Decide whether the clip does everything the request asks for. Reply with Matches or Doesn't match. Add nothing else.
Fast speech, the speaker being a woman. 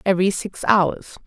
Doesn't match